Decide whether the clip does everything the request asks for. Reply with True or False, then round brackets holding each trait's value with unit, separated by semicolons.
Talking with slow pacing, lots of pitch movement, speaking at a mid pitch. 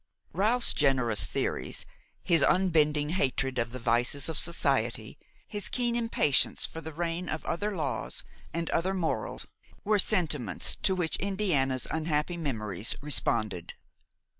True (130 wpm; 5.9 semitones; 155 Hz)